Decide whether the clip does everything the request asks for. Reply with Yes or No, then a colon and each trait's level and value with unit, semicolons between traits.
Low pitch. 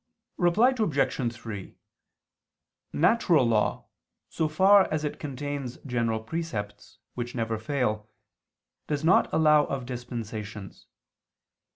Yes: low, 130 Hz